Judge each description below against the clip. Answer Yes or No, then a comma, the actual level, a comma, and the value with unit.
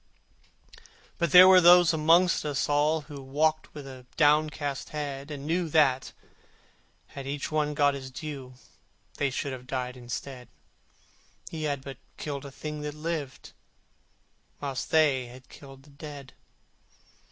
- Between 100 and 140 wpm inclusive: Yes, slow, 135 wpm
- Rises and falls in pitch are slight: Yes, narrow, 2.3 semitones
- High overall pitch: No, medium, 145 Hz